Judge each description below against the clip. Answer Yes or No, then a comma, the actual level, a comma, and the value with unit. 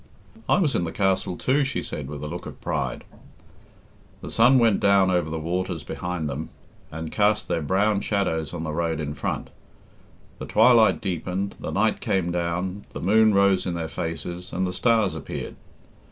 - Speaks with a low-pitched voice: Yes, very low, 90 Hz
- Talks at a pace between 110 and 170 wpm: No, average, 180 wpm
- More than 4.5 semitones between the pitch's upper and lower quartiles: No, average, 3.8 semitones